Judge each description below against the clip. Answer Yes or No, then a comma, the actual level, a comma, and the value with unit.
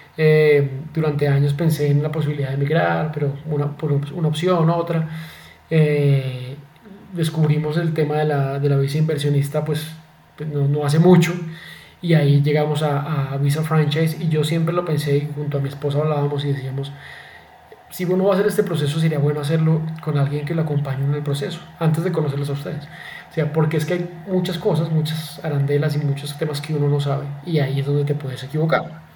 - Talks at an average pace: No, fast, 200 wpm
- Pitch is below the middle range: No, medium, 150 Hz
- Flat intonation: Yes, narrow, 2.0 semitones